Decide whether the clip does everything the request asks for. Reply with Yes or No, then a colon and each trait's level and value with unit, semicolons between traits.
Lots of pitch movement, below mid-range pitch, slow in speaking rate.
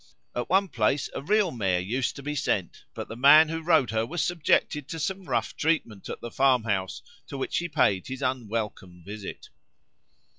No: wide, 6.8 semitones; low, 130 Hz; average, 185 wpm